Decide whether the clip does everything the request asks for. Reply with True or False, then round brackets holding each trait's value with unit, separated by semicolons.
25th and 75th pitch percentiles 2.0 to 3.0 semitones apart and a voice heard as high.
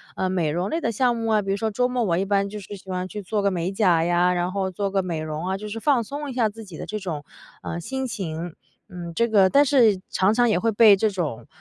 False (3.7 semitones; 195 Hz)